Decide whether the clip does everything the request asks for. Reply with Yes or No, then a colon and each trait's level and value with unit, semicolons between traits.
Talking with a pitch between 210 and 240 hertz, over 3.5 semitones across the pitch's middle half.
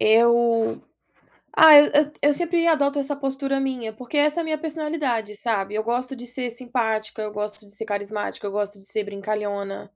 Yes: high, 235 Hz; average, 5.1 semitones